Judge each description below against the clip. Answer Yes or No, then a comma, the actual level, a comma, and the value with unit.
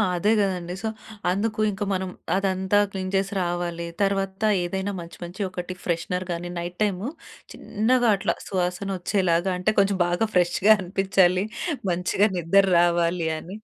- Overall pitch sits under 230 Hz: Yes, medium, 185 Hz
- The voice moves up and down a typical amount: No, narrow, 2.0 semitones